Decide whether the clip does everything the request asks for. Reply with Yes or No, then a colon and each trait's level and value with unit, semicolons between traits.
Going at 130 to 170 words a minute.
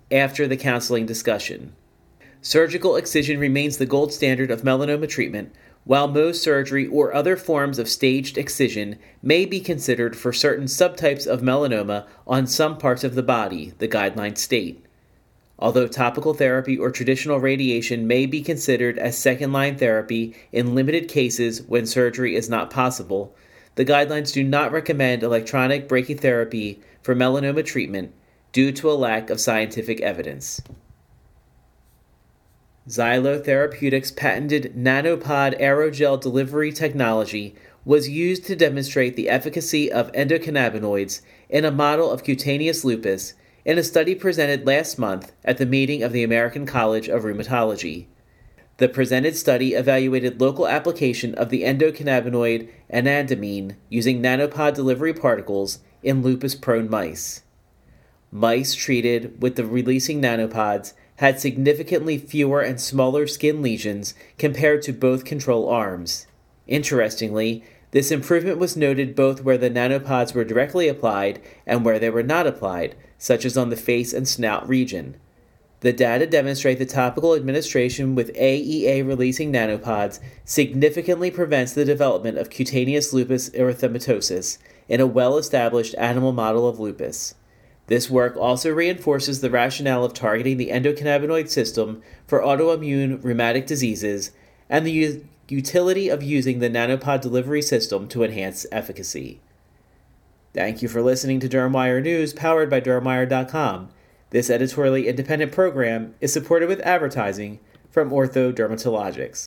Yes: slow, 135 wpm